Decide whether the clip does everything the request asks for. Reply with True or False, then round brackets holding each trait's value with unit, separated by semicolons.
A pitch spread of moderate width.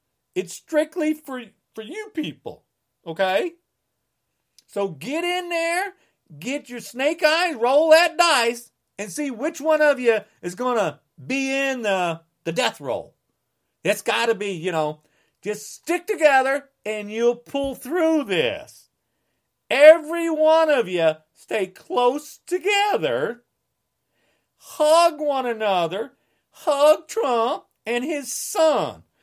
False (7.5 semitones)